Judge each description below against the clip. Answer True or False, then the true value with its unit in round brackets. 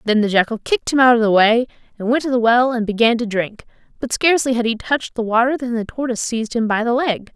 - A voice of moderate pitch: False (235 Hz)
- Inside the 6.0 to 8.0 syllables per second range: True (6.5 syllables/s)